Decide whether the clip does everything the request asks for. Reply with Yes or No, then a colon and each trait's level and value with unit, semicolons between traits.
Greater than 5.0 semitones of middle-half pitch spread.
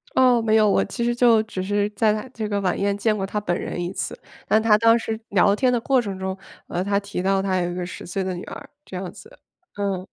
No: average, 2.8 semitones